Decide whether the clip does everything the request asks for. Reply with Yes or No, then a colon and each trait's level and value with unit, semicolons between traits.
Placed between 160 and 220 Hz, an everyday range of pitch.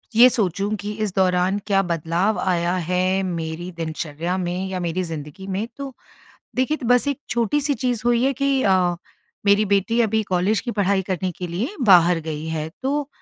Yes: high, 190 Hz; average, 5.0 semitones